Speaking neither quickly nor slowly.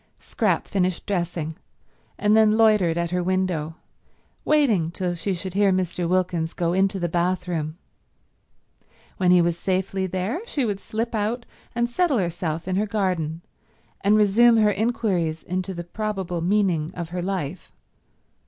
Yes: average, 150 wpm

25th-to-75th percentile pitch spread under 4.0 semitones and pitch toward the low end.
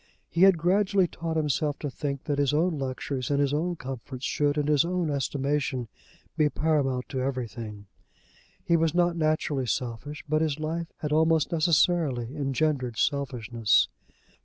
No: average, 3.4 semitones; medium, 145 Hz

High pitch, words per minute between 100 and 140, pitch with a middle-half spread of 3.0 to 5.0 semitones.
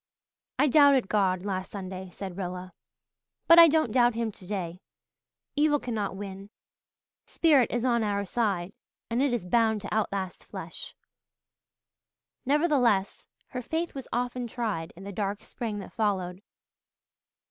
Yes: high, 210 Hz; slow, 135 wpm; average, 4.5 semitones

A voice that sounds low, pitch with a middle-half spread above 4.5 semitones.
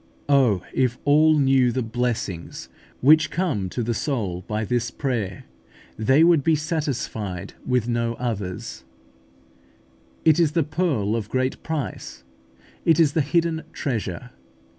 Yes: low, 125 Hz; wide, 5.5 semitones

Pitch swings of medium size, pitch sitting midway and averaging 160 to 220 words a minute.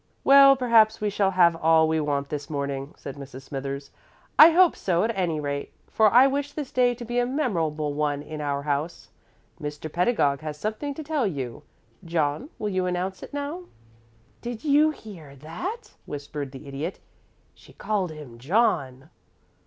No: wide, 8.8 semitones; medium, 170 Hz; average, 170 wpm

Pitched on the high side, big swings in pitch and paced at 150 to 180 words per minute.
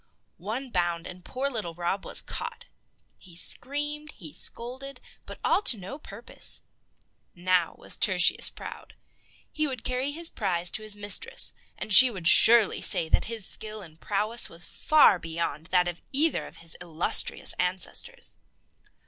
Yes: high, 205 Hz; wide, 6.6 semitones; average, 155 wpm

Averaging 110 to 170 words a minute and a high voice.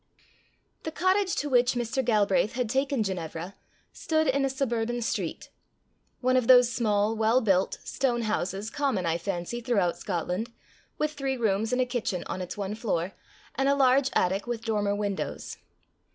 Yes: average, 165 wpm; high, 230 Hz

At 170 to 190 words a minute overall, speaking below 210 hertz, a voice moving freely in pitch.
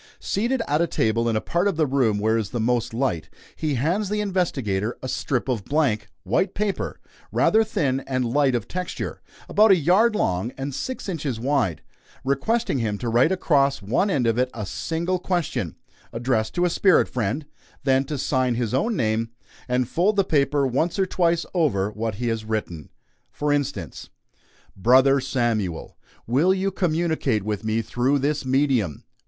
Yes: average, 175 wpm; low, 135 Hz; wide, 6.8 semitones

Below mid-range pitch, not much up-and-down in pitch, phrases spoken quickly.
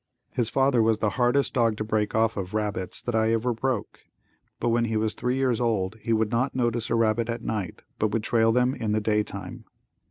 Yes: low, 115 Hz; narrow, 1.9 semitones; fast, 225 wpm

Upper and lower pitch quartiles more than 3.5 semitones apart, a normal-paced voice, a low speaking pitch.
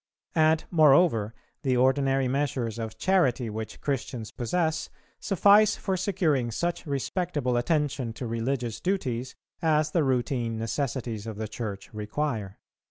No: average, 5.3 semitones; slow, 125 wpm; low, 130 Hz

